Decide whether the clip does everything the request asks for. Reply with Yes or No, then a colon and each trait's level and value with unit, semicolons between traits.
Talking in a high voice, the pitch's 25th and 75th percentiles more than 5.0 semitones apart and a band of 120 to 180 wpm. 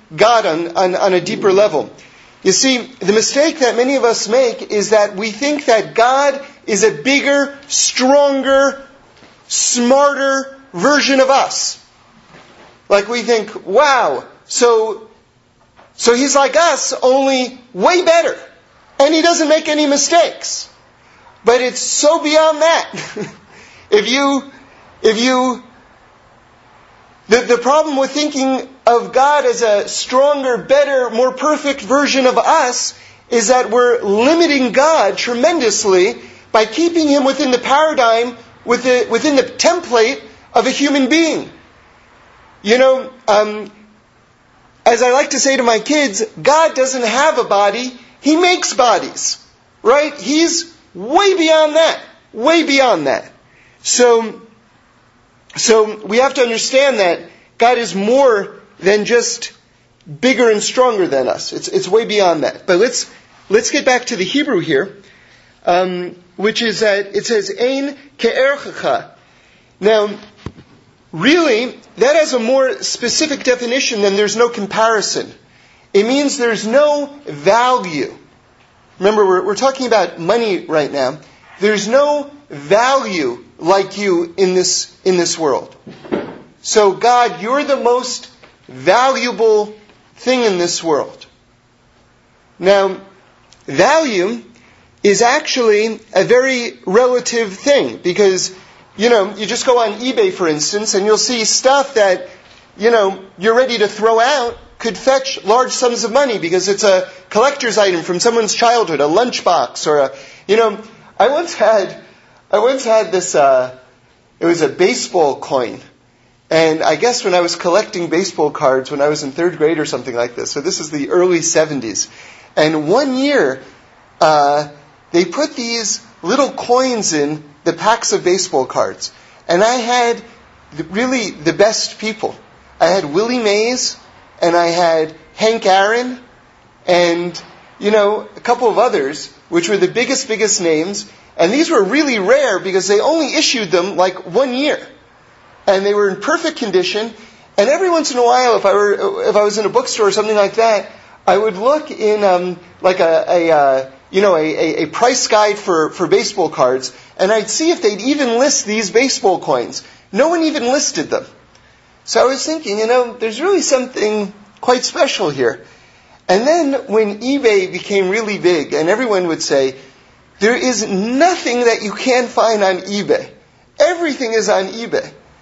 Yes: high, 230 Hz; wide, 5.5 semitones; average, 150 wpm